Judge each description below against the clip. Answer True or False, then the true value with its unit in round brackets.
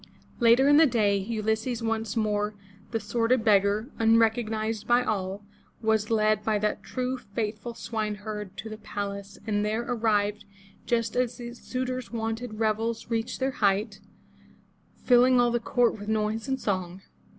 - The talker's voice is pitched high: True (220 Hz)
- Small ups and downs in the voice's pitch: True (2.3 semitones)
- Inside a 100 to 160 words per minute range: True (150 wpm)